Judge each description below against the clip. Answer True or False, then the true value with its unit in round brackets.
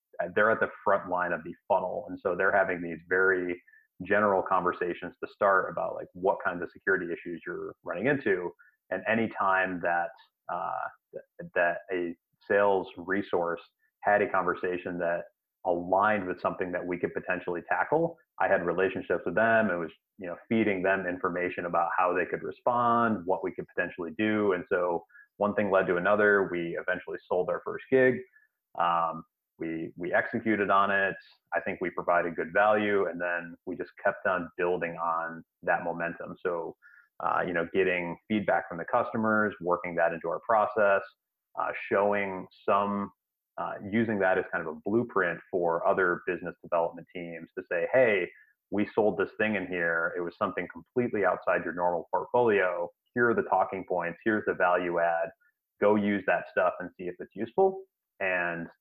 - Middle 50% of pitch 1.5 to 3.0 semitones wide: False (3.8 semitones)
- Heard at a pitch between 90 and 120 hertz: True (95 Hz)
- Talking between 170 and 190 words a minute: True (175 wpm)